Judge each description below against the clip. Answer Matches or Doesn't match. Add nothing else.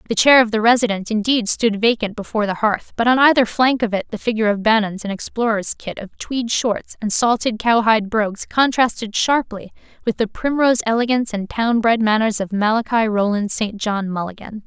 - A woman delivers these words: Matches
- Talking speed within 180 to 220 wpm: Matches